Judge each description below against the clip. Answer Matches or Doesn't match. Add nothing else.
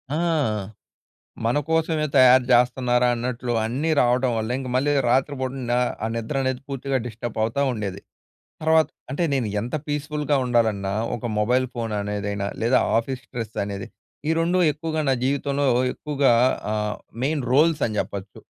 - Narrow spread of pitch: Doesn't match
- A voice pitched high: Doesn't match